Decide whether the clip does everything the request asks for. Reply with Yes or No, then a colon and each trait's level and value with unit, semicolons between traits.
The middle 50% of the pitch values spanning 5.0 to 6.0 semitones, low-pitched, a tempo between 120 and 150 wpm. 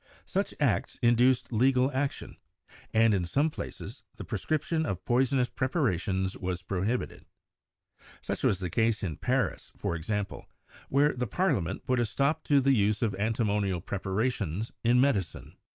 Yes: average, 5.3 semitones; low, 115 Hz; average, 145 wpm